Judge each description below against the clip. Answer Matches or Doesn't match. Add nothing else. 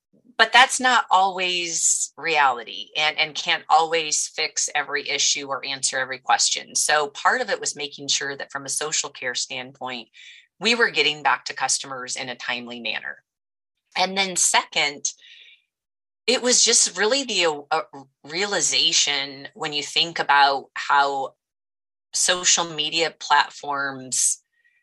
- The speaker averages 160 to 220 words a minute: Doesn't match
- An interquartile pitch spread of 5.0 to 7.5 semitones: Matches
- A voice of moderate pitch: Matches